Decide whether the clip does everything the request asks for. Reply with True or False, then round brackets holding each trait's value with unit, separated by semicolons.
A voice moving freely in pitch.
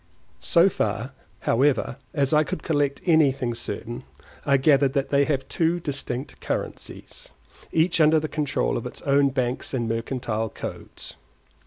False (3.6 semitones)